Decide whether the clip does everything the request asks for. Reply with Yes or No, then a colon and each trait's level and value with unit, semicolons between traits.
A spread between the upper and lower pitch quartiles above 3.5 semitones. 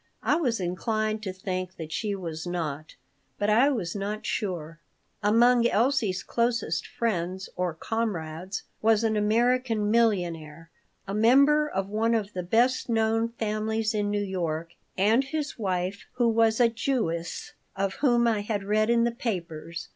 Yes: average, 4.1 semitones